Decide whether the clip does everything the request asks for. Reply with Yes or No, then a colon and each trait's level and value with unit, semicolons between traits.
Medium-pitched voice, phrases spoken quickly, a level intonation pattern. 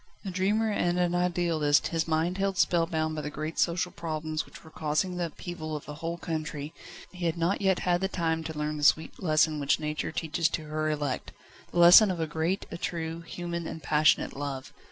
Yes: medium, 165 Hz; fast, 210 wpm; narrow, 2.2 semitones